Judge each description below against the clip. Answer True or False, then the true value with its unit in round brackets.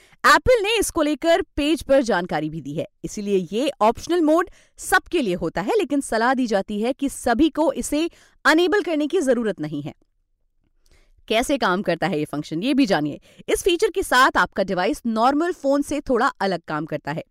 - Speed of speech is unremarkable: False (195 wpm)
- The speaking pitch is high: True (260 Hz)